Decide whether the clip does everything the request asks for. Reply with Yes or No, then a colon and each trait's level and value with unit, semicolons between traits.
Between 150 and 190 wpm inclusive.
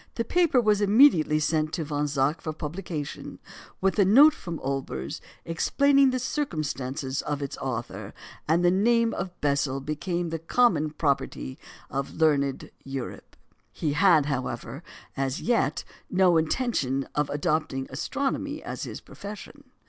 No: average, 140 wpm